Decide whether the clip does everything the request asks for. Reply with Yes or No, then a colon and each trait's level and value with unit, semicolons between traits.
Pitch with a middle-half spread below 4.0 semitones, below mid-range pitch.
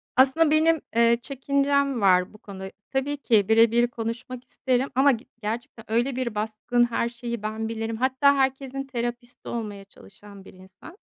No: average, 3.3 semitones; high, 240 Hz